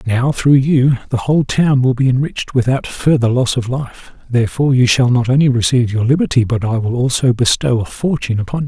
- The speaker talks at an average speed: No, fast, 215 wpm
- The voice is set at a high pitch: No, low, 125 Hz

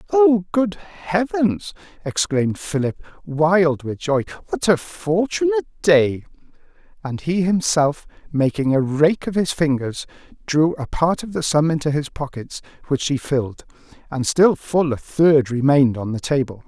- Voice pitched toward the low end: No, medium, 150 Hz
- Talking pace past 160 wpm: No, average, 150 wpm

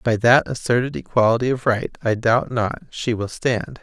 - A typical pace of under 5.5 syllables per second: Yes, 4.8 syllables/s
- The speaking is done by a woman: No, male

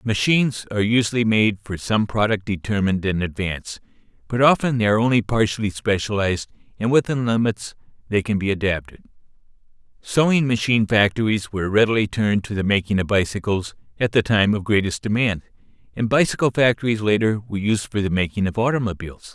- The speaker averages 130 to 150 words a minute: No, average, 160 wpm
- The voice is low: Yes, low, 105 Hz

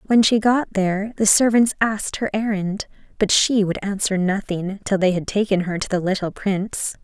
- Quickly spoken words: No, average, 195 wpm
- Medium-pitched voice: No, high, 200 Hz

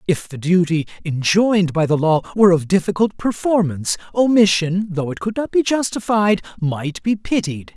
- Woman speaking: No, male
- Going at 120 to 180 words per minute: Yes, average, 160 wpm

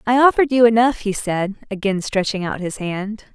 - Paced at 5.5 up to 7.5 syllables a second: No, 5.0 syllables/s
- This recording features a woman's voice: Yes, female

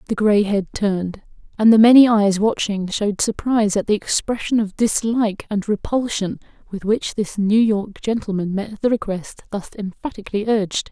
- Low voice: No, high, 210 Hz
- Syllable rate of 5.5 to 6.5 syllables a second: No, 5.1 syllables/s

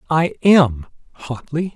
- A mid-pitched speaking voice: Yes, medium, 150 Hz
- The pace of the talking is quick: No, slow, 105 wpm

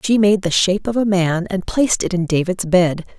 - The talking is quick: Yes, fast, 245 wpm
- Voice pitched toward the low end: No, high, 190 Hz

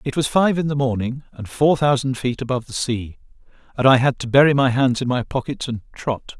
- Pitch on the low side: Yes, low, 130 Hz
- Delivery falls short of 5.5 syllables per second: No, 5.7 syllables/s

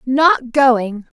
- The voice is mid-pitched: No, high, 245 Hz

